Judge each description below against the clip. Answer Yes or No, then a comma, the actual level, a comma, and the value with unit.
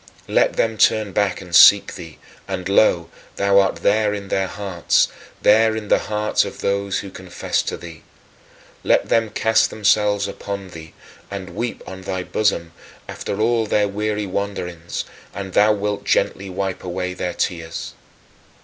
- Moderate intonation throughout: No, narrow, 2.3 semitones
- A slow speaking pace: No, average, 160 wpm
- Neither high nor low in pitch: No, low, 100 Hz